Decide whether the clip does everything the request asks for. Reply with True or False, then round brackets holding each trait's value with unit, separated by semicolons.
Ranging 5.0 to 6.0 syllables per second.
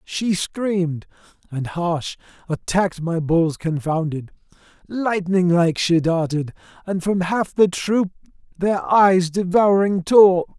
False (3.6 syllables/s)